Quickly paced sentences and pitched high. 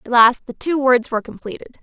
Yes: fast, 230 wpm; high, 245 Hz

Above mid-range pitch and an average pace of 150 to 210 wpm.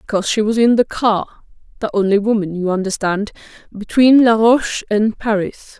No: high, 215 Hz; slow, 135 wpm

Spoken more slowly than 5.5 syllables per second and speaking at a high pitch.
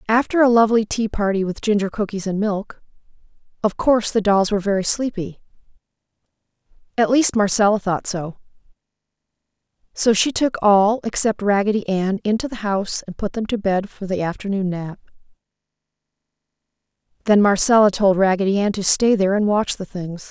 No: 5.6 syllables/s; high, 205 Hz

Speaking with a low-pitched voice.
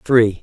Yes: low, 110 Hz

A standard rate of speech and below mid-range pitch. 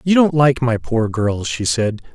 No: fast, 225 wpm; low, 125 Hz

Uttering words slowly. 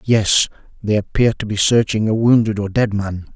No: average, 195 wpm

